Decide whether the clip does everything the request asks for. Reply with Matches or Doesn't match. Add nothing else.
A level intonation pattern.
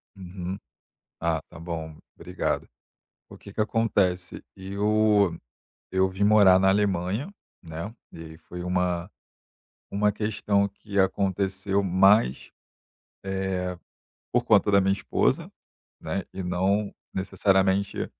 Matches